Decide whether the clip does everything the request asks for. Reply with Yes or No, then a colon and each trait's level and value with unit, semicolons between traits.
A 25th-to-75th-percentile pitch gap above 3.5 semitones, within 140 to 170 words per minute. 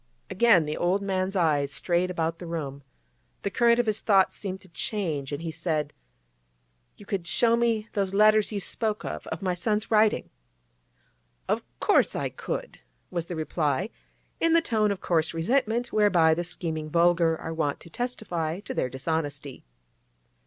Yes: average, 4.7 semitones; average, 165 wpm